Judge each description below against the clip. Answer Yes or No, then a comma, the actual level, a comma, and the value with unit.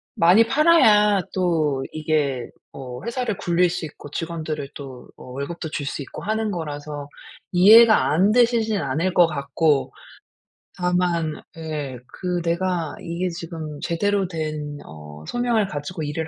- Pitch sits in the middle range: Yes, medium, 165 Hz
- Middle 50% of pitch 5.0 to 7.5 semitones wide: No, average, 4.3 semitones